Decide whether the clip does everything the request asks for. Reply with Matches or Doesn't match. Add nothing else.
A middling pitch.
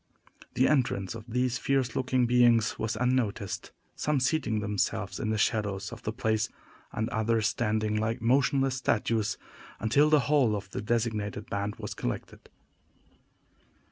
Doesn't match